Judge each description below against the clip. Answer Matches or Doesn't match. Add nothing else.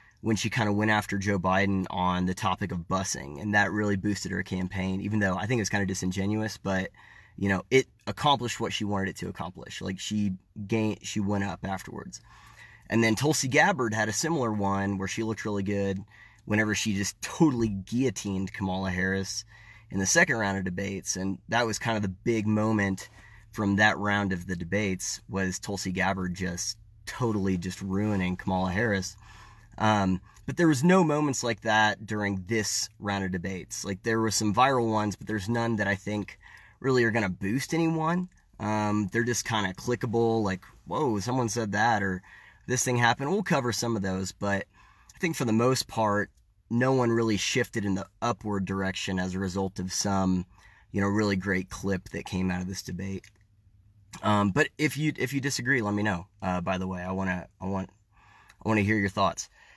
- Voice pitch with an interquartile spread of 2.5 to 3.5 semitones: Matches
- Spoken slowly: Doesn't match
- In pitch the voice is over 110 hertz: Doesn't match